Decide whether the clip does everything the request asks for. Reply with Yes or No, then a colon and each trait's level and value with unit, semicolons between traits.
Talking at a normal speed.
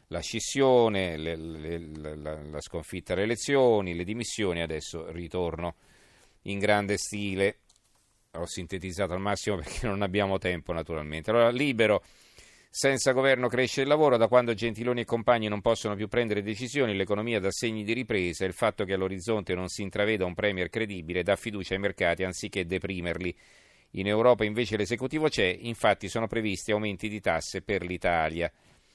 Yes: average, 155 wpm